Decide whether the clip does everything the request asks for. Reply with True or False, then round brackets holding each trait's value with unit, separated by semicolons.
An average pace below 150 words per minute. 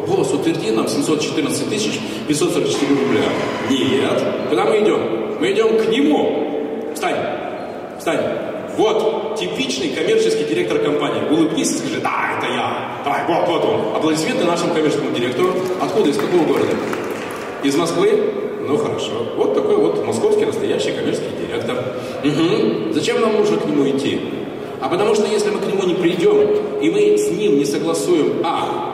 False (155 wpm)